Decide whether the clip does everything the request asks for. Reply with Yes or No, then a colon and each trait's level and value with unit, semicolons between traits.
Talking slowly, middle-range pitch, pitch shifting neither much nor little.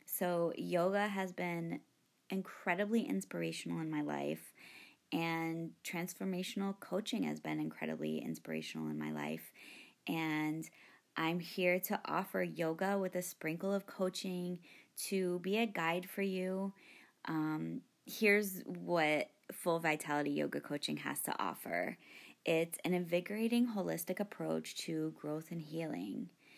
Yes: slow, 125 wpm; medium, 170 Hz; average, 4.4 semitones